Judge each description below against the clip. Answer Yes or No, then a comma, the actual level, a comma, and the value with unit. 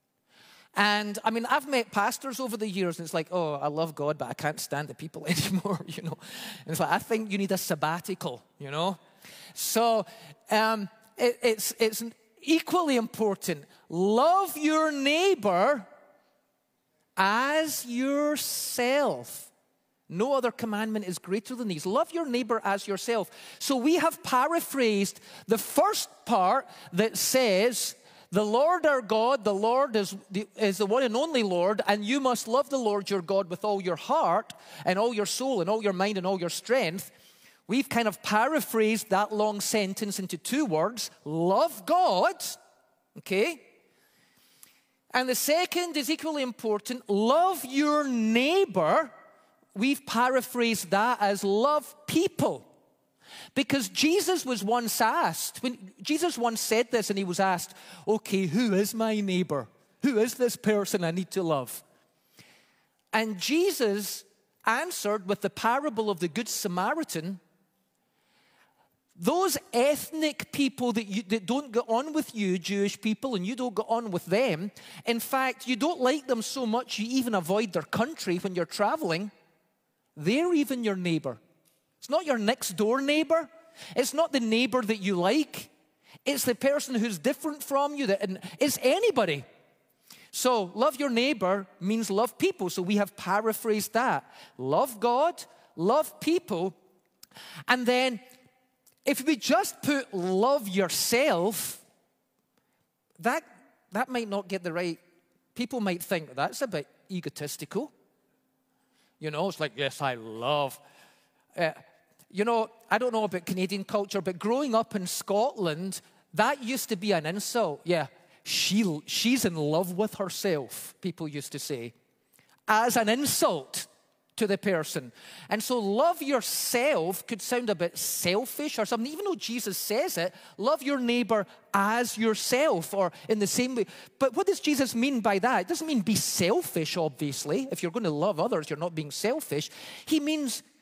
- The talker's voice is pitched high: Yes, high, 220 Hz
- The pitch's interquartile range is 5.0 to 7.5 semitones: Yes, wide, 5.6 semitones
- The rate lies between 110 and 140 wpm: No, average, 155 wpm